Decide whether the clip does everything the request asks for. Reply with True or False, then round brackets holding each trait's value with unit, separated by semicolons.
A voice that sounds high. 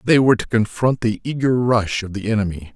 False (110 Hz)